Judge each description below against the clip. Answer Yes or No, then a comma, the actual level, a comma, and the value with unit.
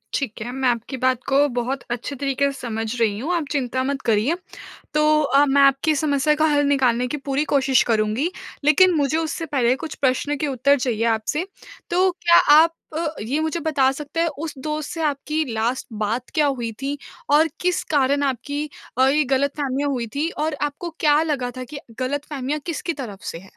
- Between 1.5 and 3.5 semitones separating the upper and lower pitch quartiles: Yes, average, 3.1 semitones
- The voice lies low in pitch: No, very high, 280 Hz